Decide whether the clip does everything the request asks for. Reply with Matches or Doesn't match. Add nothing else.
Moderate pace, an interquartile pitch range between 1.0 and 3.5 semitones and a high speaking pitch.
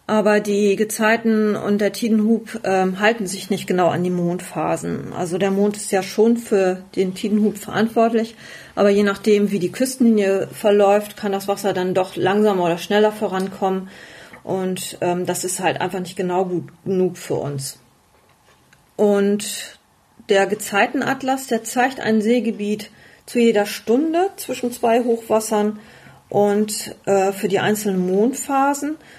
Matches